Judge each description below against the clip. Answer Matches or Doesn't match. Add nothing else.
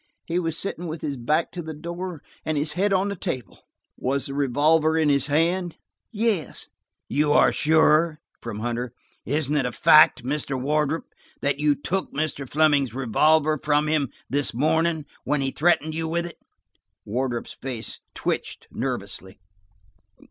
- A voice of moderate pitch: Matches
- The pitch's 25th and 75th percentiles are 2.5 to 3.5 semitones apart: Matches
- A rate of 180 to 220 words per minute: Doesn't match